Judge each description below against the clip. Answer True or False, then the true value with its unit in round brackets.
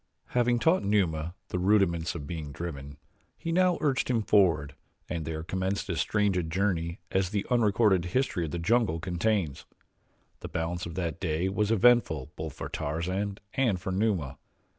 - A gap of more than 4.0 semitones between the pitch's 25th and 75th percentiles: True (4.4 semitones)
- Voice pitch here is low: True (90 Hz)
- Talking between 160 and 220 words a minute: True (165 wpm)